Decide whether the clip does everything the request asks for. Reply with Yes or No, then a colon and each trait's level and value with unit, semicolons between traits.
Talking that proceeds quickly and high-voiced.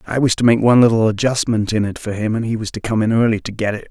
No: fast, 325 wpm; low, 110 Hz